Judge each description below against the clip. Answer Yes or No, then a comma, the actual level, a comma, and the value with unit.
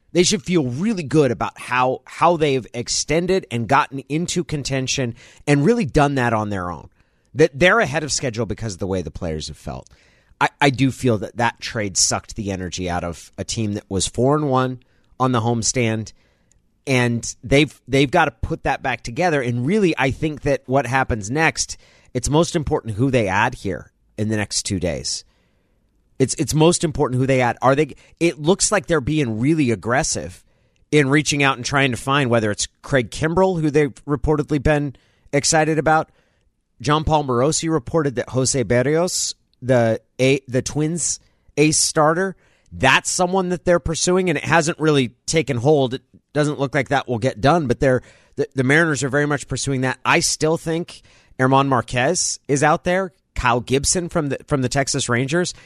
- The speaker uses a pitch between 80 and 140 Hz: Yes, low, 135 Hz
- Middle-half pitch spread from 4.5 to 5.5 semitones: Yes, average, 4.8 semitones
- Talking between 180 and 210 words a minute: Yes, average, 190 wpm